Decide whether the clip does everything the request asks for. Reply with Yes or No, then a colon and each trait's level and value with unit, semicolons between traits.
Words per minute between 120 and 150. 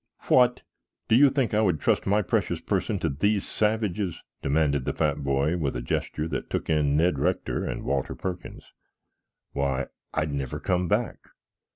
No: average, 170 wpm